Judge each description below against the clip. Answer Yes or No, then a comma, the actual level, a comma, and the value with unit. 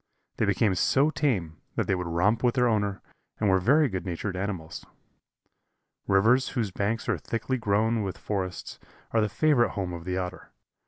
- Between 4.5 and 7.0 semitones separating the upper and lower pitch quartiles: No, average, 4.0 semitones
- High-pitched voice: No, low, 100 Hz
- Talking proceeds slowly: No, average, 175 wpm